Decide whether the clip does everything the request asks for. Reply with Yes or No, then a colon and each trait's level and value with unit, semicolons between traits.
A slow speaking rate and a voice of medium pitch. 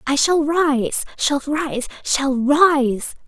No: slow, 130 wpm; very high, 285 Hz